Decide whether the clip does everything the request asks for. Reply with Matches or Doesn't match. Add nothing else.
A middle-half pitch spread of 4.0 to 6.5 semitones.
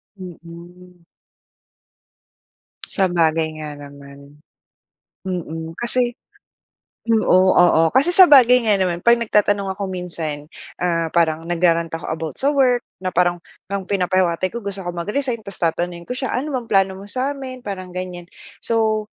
Matches